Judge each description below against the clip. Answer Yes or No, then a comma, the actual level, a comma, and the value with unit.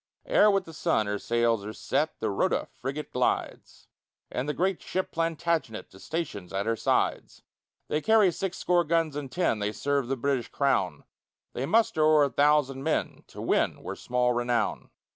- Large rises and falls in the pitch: Yes, wide, 5.9 semitones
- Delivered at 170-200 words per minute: Yes, average, 180 wpm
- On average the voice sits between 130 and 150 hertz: Yes, medium, 140 Hz